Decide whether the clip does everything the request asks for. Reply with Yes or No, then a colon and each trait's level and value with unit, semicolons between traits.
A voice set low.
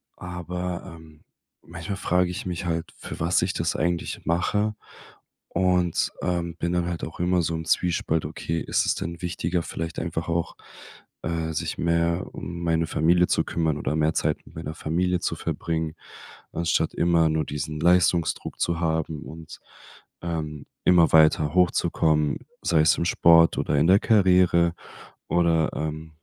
Yes: very low, 85 Hz